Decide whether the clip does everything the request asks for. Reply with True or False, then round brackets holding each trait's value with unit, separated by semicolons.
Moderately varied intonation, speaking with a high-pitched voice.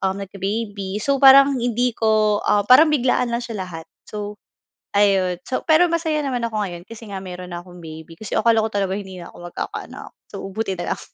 True (4.3 semitones; 210 Hz)